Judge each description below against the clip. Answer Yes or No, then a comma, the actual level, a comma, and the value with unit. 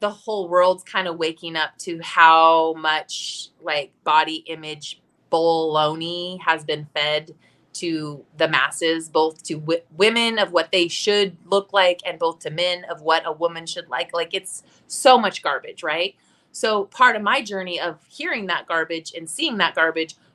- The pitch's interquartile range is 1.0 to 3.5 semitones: Yes, average, 2.9 semitones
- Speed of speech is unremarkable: Yes, average, 175 wpm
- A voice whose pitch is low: No, medium, 170 Hz